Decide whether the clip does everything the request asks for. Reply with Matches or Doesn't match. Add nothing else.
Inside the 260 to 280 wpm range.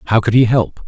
Matches